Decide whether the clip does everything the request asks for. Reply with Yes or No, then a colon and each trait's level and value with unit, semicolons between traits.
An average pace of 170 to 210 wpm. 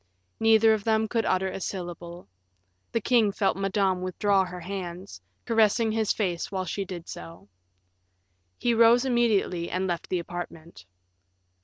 No: average, 145 wpm